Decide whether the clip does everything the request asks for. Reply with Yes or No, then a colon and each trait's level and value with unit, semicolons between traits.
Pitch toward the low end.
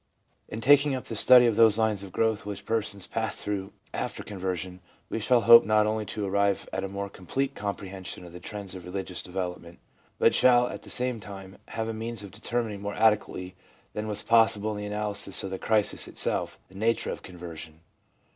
Yes: low, 105 Hz